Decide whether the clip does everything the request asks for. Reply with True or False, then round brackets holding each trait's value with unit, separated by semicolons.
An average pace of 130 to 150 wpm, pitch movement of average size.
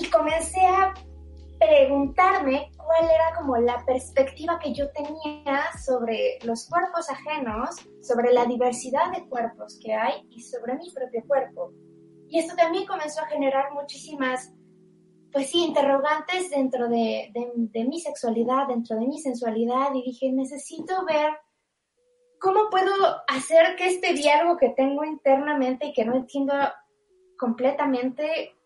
True (140 wpm; 4.7 semitones)